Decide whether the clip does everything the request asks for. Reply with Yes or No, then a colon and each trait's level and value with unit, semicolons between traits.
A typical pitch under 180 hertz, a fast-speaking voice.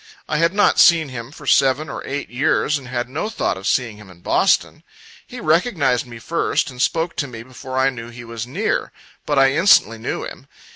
Yes: low, 135 Hz; fast, 210 wpm